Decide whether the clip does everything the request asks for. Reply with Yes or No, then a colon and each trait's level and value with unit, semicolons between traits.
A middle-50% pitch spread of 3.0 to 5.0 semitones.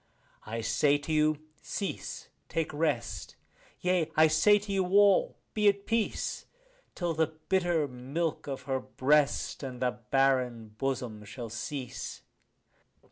No: wide, 5.5 semitones